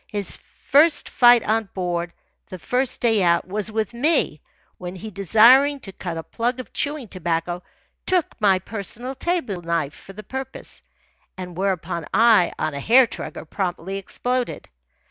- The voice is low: No, high, 205 Hz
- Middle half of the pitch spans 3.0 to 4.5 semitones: No, wide, 5.5 semitones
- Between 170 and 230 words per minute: No, average, 155 wpm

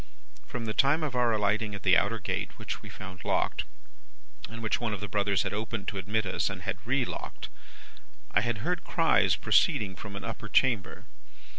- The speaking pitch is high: No, low, 110 Hz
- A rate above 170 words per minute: Yes, average, 190 wpm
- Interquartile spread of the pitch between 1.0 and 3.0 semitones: Yes, average, 2.7 semitones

